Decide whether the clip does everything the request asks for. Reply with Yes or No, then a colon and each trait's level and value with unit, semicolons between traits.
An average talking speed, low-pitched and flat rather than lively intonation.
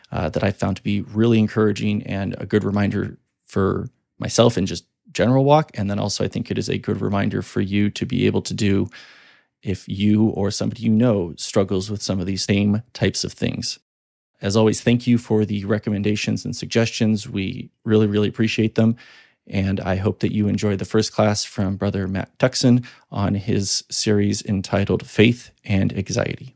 Yes: average, 190 wpm; low, 105 Hz; narrow, 2.3 semitones